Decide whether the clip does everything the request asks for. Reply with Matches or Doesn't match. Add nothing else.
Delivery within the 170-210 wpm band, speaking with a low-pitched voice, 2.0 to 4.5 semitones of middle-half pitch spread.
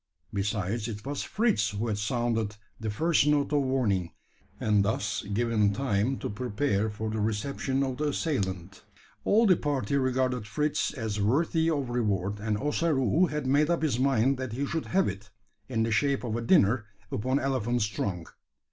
Doesn't match